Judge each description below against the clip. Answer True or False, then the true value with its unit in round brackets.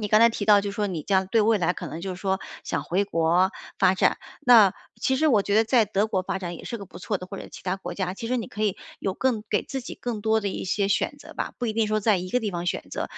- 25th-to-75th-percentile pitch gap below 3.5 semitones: True (2.7 semitones)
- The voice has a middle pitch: False (205 Hz)